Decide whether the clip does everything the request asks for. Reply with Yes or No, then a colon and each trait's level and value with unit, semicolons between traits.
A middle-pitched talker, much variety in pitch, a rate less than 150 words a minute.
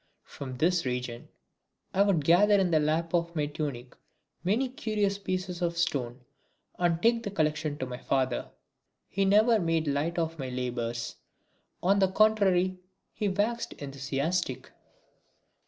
Yes: medium, 170 Hz; wide, 5.9 semitones; average, 140 wpm